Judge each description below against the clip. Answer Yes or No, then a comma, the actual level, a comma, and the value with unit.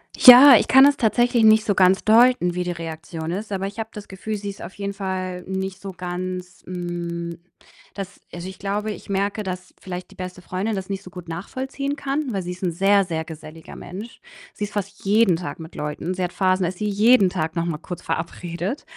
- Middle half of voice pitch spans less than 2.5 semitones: No, average, 2.9 semitones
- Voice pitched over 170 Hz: Yes, high, 190 Hz